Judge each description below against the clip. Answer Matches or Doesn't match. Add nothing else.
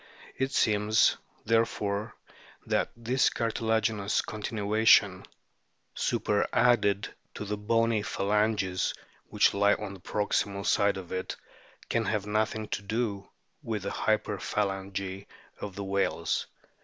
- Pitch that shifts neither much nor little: Doesn't match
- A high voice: Doesn't match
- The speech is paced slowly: Matches